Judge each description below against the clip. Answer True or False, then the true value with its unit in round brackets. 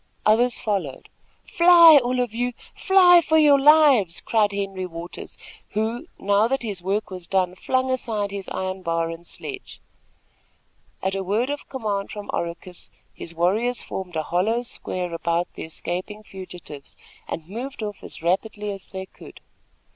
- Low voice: False (205 Hz)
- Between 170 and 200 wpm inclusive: False (155 wpm)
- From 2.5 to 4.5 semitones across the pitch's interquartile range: False (5.3 semitones)